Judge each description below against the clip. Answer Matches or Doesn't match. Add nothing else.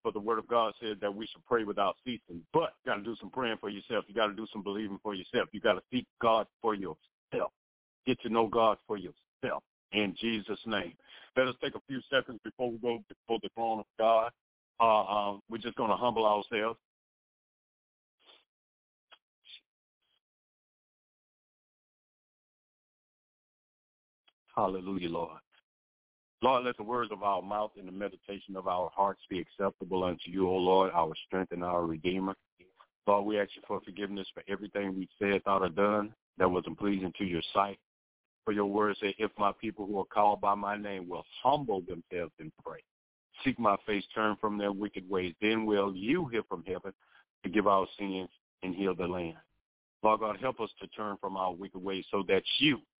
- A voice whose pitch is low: Matches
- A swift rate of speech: Doesn't match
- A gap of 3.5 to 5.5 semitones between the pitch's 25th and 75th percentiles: Doesn't match